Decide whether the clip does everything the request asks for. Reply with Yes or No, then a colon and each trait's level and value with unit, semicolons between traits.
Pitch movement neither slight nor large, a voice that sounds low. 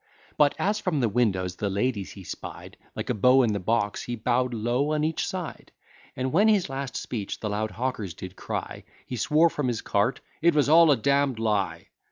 No: wide, 5.7 semitones; low, 125 Hz